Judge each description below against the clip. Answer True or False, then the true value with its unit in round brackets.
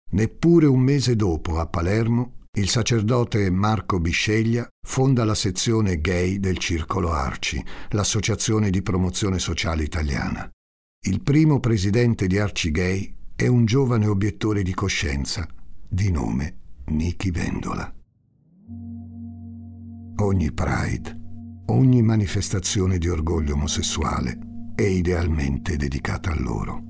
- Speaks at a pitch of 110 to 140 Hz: False (100 Hz)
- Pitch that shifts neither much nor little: True (4.7 semitones)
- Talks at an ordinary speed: False (110 wpm)